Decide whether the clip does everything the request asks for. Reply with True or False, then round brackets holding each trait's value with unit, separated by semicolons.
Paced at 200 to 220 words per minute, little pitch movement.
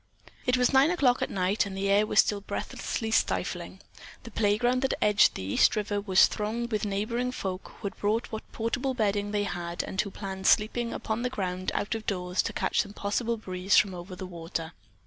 False (205 wpm; 3.3 semitones)